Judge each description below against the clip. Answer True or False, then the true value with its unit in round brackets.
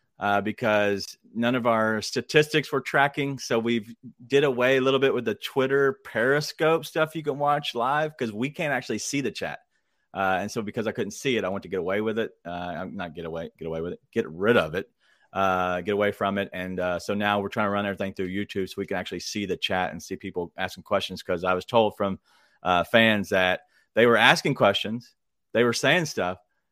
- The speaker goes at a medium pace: False (235 wpm)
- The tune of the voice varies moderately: False (5.7 semitones)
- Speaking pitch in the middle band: False (110 Hz)